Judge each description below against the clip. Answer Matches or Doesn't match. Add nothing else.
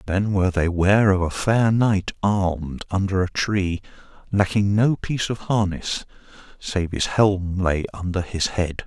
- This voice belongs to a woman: Doesn't match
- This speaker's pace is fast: Doesn't match